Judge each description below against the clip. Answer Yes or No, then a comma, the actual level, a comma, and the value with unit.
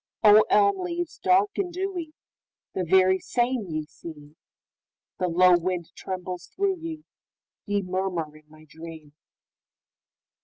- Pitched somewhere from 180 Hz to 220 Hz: Yes, high, 190 Hz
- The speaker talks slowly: Yes, slow, 110 wpm